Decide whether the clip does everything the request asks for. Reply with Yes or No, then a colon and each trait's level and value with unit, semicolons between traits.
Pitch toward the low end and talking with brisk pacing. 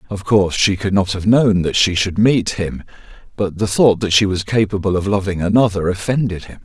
Yes: low, 100 Hz; fast, 215 wpm